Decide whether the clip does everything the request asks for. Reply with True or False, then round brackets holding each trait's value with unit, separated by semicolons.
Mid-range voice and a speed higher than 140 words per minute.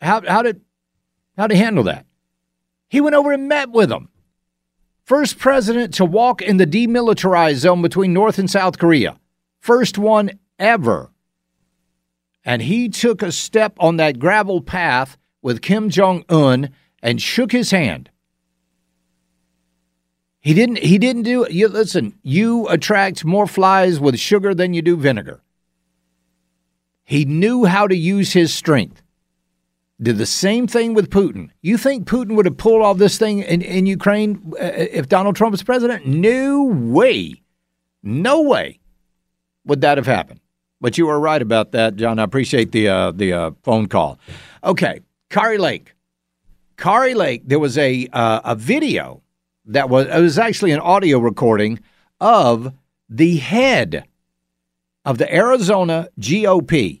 True (165 Hz; 150 wpm)